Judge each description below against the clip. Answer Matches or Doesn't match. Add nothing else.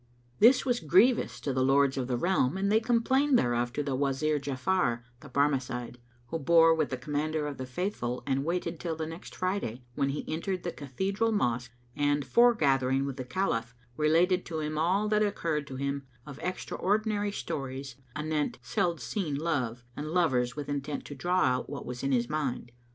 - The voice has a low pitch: Doesn't match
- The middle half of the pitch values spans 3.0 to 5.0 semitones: Doesn't match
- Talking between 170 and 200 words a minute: Matches